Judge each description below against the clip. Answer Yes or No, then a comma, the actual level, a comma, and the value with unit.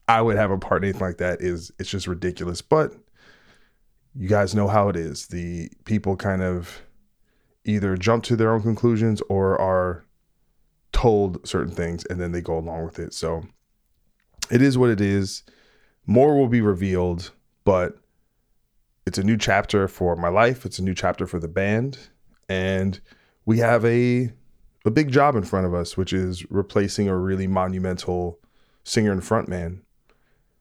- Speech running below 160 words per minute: No, average, 170 wpm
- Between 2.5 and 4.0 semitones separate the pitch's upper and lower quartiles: Yes, average, 3.3 semitones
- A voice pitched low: Yes, very low, 95 Hz